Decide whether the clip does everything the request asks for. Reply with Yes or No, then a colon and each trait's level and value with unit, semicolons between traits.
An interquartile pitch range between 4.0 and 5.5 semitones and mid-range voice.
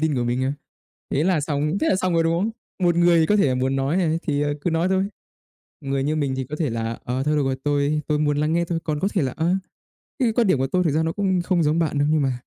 No: average, 3.6 semitones; medium, 155 Hz